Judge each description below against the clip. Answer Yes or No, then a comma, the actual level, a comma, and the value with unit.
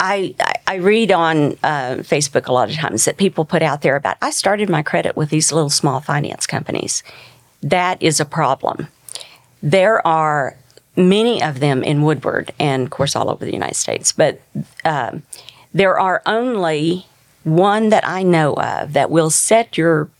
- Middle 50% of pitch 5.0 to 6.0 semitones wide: No, average, 4.0 semitones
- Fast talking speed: No, average, 175 wpm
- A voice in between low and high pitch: Yes, medium, 160 Hz